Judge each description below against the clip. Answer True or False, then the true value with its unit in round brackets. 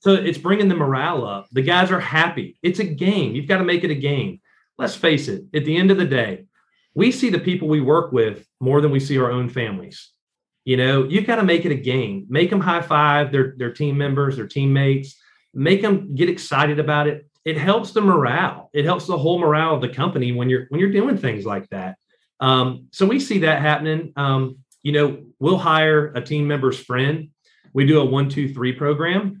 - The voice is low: False (150 Hz)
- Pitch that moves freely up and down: False (4.6 semitones)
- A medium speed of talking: False (225 wpm)